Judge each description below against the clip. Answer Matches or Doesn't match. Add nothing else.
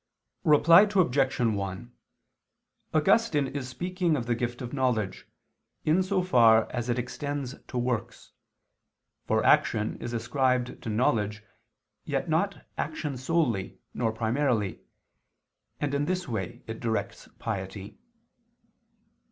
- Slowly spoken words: Matches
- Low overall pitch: Matches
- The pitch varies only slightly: Doesn't match